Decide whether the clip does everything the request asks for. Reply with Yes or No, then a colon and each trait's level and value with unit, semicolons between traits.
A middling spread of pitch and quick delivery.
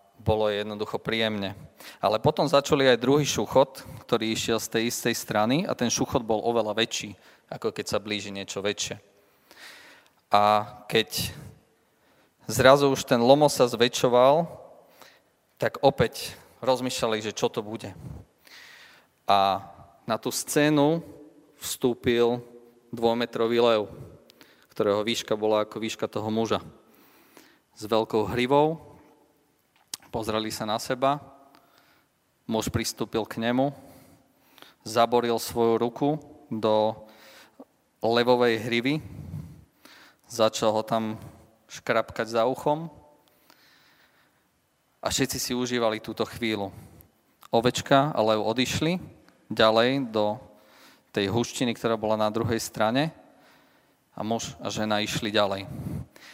No: average, 3.3 semitones; slow, 110 wpm